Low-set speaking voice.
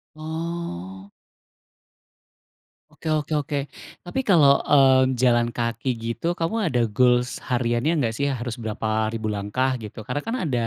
Yes: low, 125 Hz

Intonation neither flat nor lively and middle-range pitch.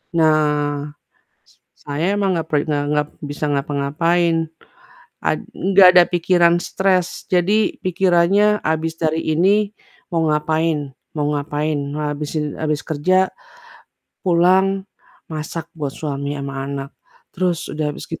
Yes: average, 3.4 semitones; medium, 160 Hz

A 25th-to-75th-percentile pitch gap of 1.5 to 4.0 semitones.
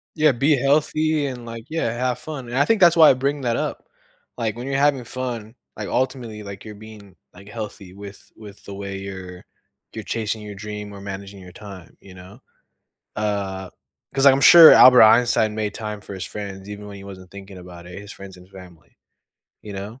No: average, 4.4 semitones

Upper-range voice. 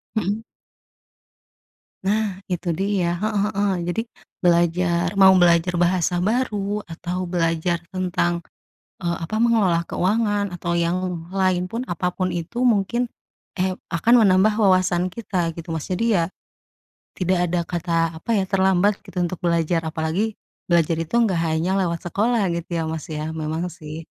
No: medium, 180 Hz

